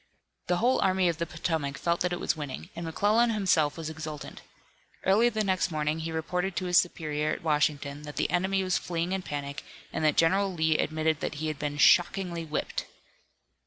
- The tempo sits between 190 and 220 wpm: Yes, average, 200 wpm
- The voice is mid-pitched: Yes, medium, 165 Hz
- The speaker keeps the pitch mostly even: No, average, 3.3 semitones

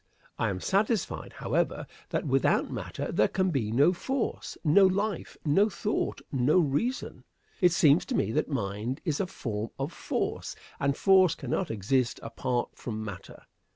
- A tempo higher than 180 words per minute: No, average, 155 wpm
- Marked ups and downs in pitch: Yes, wide, 7.7 semitones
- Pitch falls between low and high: Yes, medium, 145 Hz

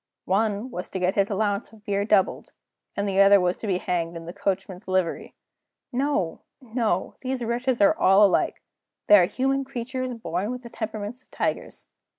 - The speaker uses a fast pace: No, average, 180 wpm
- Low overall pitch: No, high, 205 Hz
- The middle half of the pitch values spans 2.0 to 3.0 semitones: No, average, 4.3 semitones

